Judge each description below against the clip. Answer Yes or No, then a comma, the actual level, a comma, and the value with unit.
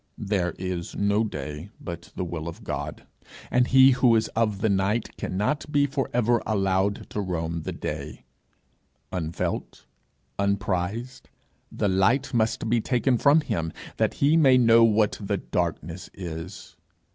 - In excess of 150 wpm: No, average, 145 wpm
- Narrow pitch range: No, average, 5.1 semitones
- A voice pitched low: Yes, low, 100 Hz